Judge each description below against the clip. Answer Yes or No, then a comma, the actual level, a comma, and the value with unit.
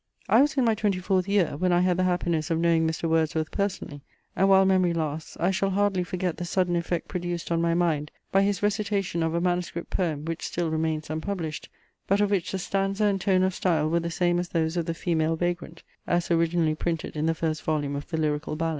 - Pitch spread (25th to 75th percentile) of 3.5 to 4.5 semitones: No, average, 2.7 semitones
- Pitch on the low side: No, medium, 175 Hz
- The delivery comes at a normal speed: No, fast, 230 wpm